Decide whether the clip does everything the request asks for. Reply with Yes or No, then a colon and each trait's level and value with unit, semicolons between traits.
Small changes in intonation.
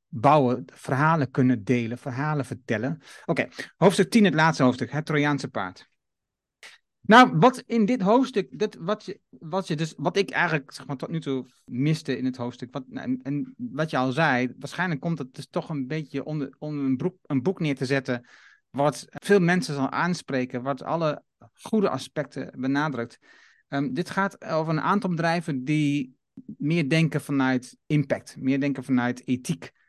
No: average, 4.4 semitones